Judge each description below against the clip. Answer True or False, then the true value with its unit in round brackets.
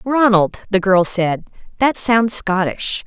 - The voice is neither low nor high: False (205 Hz)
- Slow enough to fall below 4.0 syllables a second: True (3.5 syllables/s)